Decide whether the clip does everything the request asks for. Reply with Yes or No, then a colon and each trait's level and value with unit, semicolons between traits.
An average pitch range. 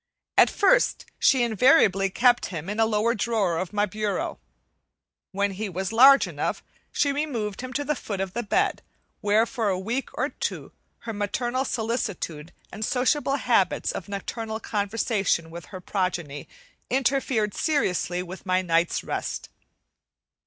Yes: average, 4.5 semitones